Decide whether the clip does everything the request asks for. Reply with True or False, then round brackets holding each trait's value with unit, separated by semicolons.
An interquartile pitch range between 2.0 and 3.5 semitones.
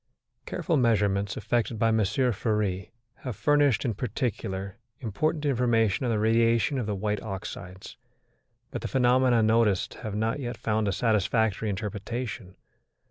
True (3.1 semitones)